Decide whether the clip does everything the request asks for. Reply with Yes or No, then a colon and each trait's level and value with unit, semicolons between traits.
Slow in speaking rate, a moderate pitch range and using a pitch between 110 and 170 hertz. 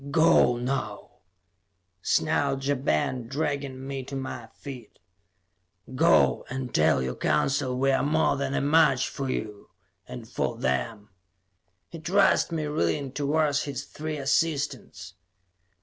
Yes: slow, 130 wpm; average, 3.2 semitones; low, 135 Hz